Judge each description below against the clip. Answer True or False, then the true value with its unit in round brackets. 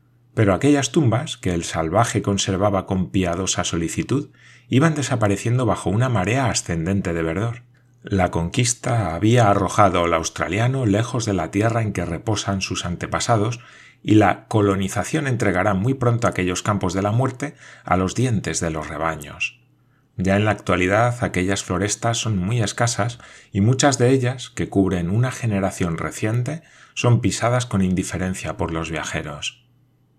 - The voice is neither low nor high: False (105 Hz)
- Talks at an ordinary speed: True (150 wpm)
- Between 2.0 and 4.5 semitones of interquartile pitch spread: False (4.9 semitones)